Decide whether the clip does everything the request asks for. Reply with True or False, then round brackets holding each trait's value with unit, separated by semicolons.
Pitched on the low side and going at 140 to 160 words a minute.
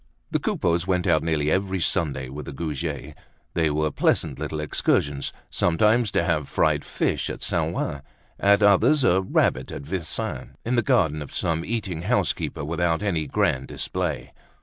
False (80 Hz; 170 wpm)